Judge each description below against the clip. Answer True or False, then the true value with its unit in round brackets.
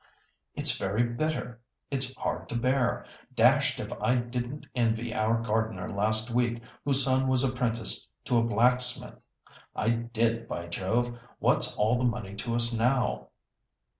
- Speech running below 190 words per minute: True (145 wpm)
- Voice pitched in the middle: False (120 Hz)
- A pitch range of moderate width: False (1.8 semitones)